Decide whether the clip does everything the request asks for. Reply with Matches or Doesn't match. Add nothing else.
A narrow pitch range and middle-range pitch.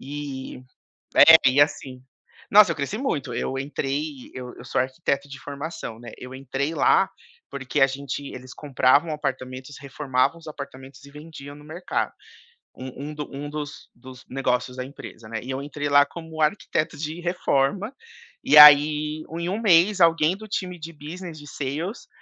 Doesn't match